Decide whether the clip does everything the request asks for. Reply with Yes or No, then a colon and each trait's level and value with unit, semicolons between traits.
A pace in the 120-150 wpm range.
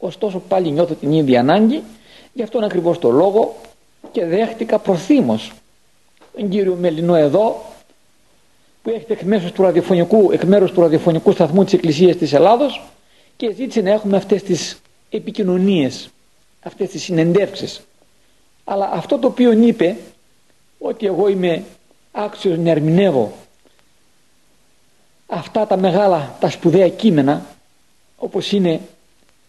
Yes: average, 125 wpm